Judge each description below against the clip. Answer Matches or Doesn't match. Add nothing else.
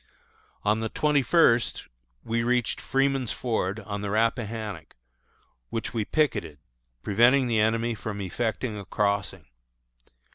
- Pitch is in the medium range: Doesn't match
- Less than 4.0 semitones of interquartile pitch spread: Matches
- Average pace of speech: Doesn't match